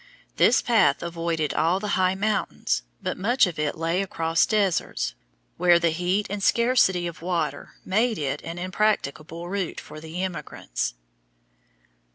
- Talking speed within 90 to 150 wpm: Yes, average, 145 wpm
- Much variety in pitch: No, average, 3.3 semitones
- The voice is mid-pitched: Yes, medium, 180 Hz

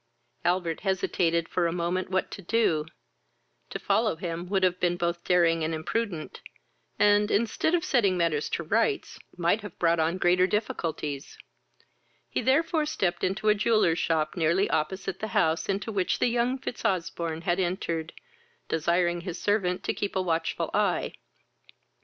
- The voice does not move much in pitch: No, average, 3.5 semitones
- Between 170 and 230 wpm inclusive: No, average, 155 wpm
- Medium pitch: Yes, medium, 180 Hz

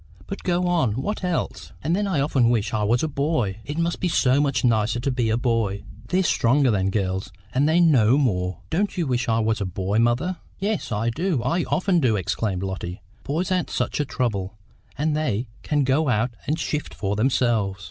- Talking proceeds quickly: Yes, fast, 210 wpm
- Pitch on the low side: Yes, low, 125 Hz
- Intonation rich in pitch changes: Yes, wide, 6.6 semitones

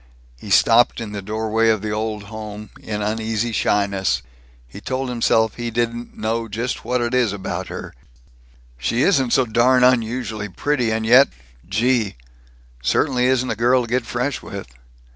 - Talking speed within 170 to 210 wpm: No, average, 160 wpm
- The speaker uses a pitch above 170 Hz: No, low, 115 Hz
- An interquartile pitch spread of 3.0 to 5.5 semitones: No, narrow, 2.5 semitones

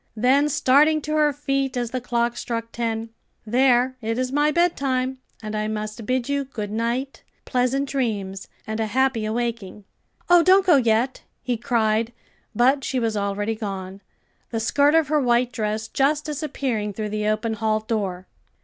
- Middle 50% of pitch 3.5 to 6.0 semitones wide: Yes, average, 3.9 semitones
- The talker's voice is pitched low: No, high, 240 Hz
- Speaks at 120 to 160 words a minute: No, average, 170 wpm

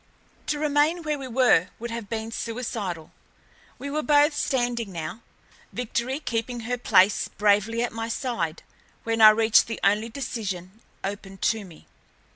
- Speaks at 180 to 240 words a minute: No, average, 150 wpm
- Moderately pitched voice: No, high, 230 Hz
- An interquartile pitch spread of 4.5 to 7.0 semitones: No, average, 3.6 semitones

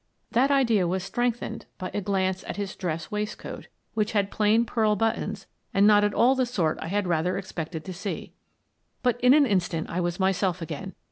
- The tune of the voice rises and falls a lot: No, average, 3.6 semitones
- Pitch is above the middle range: Yes, high, 200 Hz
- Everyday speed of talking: Yes, average, 195 wpm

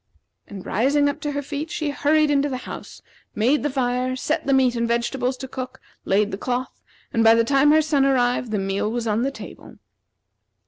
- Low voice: No, very high, 255 Hz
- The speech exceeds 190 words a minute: Yes, average, 200 wpm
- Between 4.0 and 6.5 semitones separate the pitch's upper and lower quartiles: No, average, 3.5 semitones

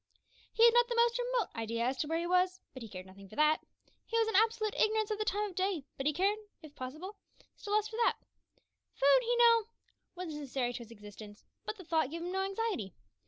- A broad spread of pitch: Yes, wide, 8.5 semitones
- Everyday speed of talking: No, fast, 235 wpm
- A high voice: Yes, very high, 365 Hz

